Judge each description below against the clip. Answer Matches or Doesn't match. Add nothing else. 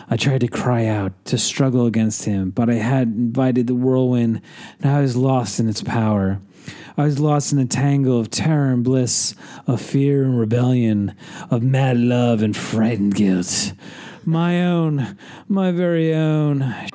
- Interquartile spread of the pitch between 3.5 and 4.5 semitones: Matches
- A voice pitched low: Matches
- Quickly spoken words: Doesn't match